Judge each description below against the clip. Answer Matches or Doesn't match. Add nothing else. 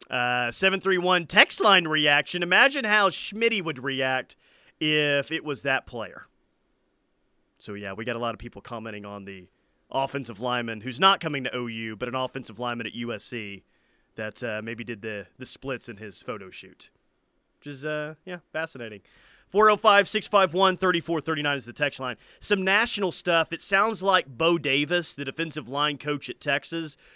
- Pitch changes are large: Matches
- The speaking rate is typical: Matches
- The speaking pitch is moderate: Matches